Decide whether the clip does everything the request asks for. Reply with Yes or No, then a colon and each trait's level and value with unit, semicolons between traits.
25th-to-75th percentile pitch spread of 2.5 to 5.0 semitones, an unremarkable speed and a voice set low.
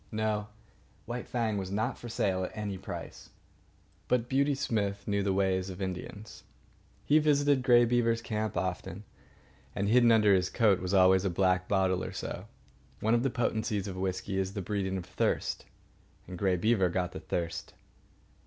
Yes: average, 3.5 semitones; average, 170 wpm; low, 100 Hz